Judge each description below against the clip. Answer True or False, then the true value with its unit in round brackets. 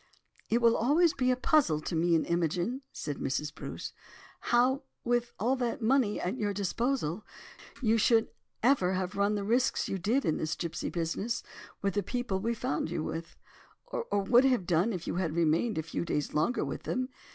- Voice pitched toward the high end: True (205 Hz)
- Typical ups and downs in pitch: False (6.2 semitones)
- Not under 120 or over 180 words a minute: False (190 wpm)